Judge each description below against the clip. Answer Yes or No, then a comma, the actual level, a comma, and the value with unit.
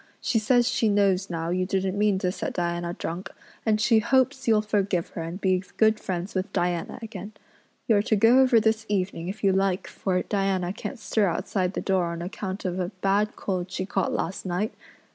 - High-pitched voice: Yes, high, 195 Hz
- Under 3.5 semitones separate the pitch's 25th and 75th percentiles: Yes, average, 2.8 semitones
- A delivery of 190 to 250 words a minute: Yes, average, 200 wpm